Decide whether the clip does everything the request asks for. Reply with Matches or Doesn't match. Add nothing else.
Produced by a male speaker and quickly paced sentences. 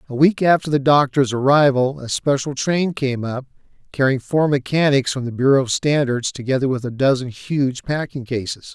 Doesn't match